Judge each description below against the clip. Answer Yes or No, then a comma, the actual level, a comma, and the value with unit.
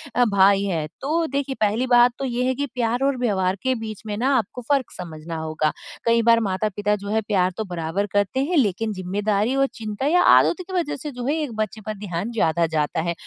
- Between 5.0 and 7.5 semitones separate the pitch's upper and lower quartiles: Yes, average, 5.3 semitones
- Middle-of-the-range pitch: No, high, 215 Hz